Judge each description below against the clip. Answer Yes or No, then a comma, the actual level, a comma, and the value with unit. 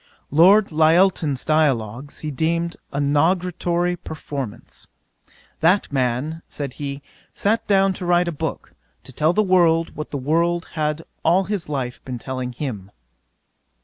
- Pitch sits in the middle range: Yes, medium, 155 Hz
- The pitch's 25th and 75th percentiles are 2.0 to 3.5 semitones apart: No, average, 4.0 semitones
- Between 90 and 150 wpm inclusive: Yes, average, 140 wpm